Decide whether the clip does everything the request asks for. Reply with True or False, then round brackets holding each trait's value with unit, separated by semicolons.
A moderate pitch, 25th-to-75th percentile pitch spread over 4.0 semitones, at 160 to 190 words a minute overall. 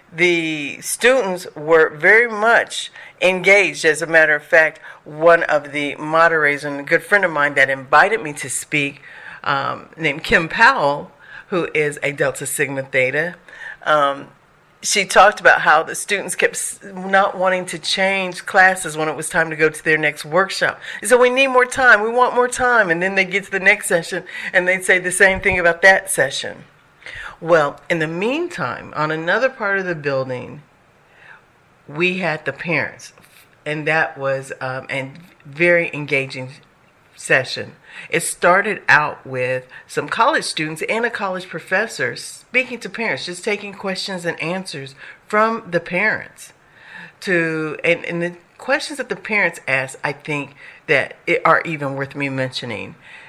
True (170 Hz; 4.7 semitones; 165 wpm)